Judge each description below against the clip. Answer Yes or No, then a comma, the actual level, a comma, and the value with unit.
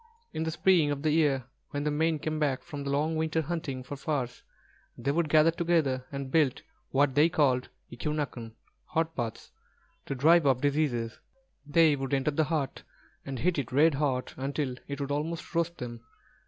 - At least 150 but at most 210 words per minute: Yes, average, 185 wpm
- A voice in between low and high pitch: Yes, medium, 145 Hz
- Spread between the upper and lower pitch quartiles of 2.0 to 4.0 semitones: Yes, average, 2.9 semitones